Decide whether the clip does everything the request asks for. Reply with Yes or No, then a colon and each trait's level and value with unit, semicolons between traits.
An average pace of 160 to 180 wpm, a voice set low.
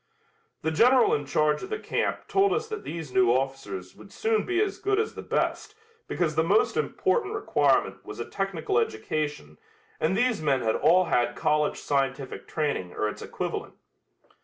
No: average, 175 wpm; medium, 155 Hz